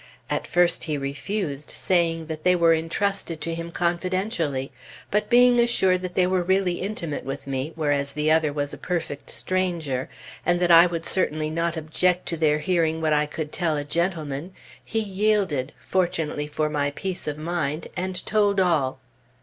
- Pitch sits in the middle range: Yes, medium, 165 Hz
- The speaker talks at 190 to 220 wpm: No, average, 175 wpm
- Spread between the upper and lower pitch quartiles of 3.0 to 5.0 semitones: Yes, average, 3.4 semitones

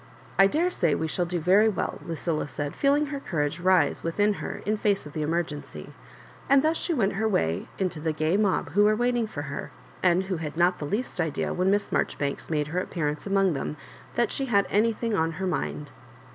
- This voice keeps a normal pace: No, fast, 215 wpm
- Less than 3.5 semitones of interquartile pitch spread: No, average, 5.2 semitones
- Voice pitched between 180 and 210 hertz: Yes, medium, 185 Hz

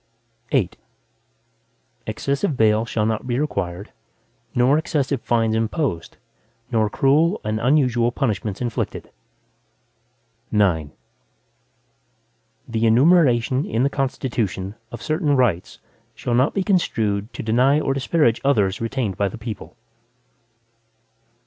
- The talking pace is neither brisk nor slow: No, slow, 110 wpm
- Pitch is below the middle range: Yes, low, 120 Hz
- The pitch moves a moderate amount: Yes, average, 4.3 semitones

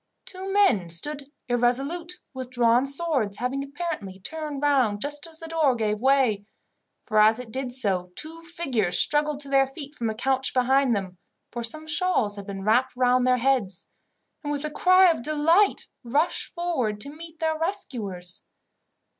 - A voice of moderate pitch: No, very high, 270 Hz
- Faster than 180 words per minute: No, average, 170 wpm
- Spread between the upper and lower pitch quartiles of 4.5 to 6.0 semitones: Yes, wide, 5.5 semitones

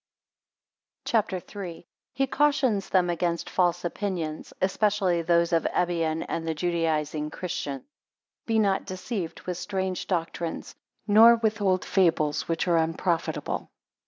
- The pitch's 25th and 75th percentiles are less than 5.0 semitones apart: Yes, average, 3.4 semitones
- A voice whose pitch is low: No, medium, 180 Hz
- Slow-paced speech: Yes, slow, 130 wpm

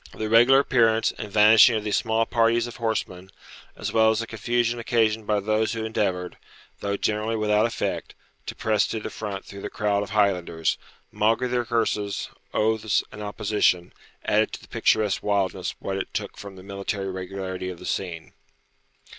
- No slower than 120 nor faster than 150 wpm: No, average, 175 wpm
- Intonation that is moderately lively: No, narrow, 2.3 semitones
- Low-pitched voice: Yes, low, 105 Hz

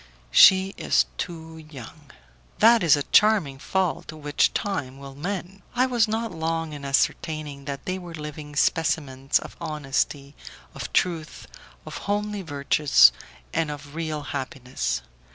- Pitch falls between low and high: Yes, medium, 155 Hz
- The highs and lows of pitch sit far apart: No, average, 4.5 semitones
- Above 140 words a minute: No, slow, 135 wpm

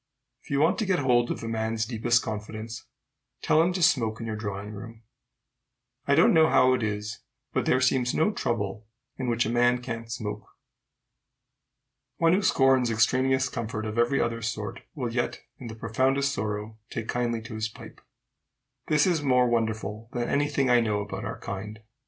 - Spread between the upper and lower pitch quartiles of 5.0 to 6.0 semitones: No, average, 3.0 semitones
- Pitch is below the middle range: Yes, low, 115 Hz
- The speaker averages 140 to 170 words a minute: No, average, 185 wpm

